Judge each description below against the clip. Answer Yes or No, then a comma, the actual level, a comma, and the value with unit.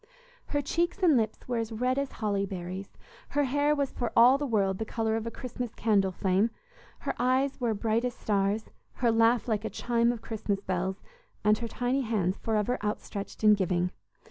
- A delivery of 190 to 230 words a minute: Yes, average, 195 wpm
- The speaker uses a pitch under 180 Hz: No, high, 225 Hz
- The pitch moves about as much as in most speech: Yes, average, 3.6 semitones